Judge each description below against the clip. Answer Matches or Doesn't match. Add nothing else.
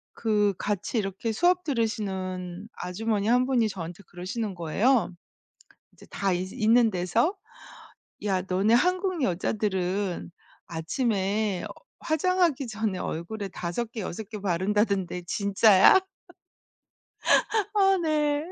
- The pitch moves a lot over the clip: Doesn't match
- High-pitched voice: Matches